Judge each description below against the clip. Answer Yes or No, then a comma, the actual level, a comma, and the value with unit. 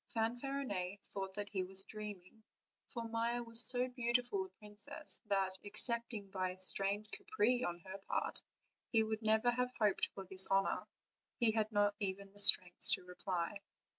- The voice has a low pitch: No, high, 210 Hz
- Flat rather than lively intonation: No, average, 3.3 semitones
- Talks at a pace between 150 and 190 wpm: Yes, average, 165 wpm